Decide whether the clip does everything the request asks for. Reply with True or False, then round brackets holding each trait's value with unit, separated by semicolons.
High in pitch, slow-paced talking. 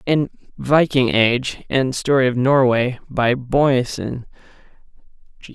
False (130 Hz; 110 wpm)